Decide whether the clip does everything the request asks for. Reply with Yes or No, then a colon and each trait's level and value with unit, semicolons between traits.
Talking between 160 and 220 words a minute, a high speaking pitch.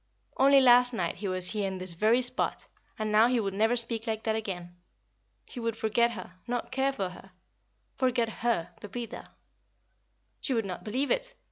Yes: average, 180 wpm; high, 225 Hz